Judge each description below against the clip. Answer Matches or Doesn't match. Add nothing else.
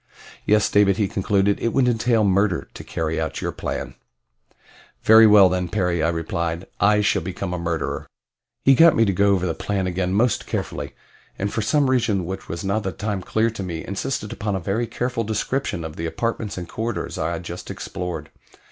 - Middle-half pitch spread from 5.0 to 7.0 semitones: Doesn't match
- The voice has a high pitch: Doesn't match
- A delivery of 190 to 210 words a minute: Matches